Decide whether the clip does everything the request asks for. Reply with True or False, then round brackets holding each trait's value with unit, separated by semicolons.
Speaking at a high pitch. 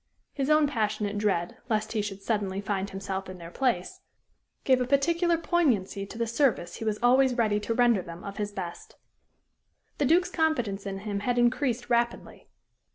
True (220 Hz)